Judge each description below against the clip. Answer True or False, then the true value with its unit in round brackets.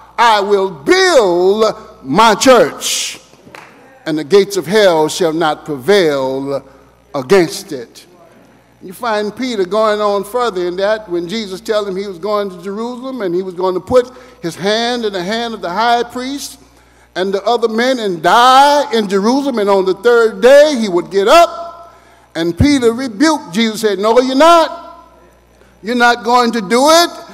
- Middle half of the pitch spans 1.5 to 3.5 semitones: False (4.8 semitones)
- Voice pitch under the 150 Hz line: False (220 Hz)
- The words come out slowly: False (170 wpm)